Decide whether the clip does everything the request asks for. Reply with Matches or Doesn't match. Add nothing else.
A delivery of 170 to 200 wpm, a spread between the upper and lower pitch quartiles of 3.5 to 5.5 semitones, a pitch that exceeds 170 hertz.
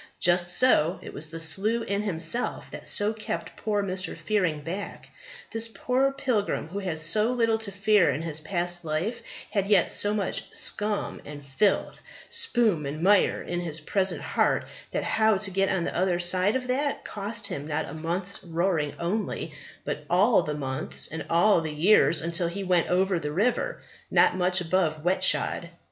Matches